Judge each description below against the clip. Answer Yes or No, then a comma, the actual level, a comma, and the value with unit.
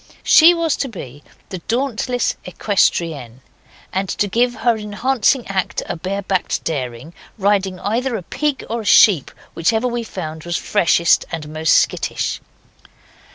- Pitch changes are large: Yes, wide, 6.0 semitones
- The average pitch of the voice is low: No, high, 200 Hz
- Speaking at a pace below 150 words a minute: Yes, average, 140 wpm